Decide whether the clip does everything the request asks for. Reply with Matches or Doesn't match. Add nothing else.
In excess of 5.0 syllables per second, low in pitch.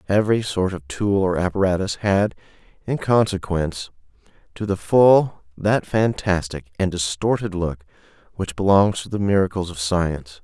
Doesn't match